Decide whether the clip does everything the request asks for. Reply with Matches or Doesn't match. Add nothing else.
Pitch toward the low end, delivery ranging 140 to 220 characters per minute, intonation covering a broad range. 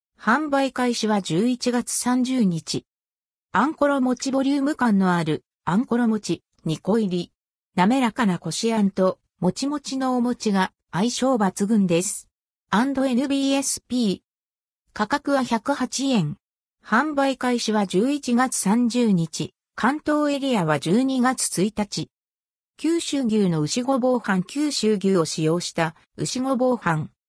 Doesn't match